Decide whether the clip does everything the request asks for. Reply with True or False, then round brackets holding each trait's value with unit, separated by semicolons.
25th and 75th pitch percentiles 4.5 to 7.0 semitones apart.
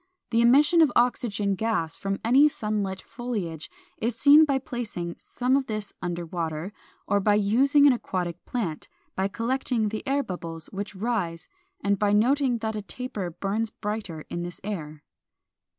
True (5.1 semitones)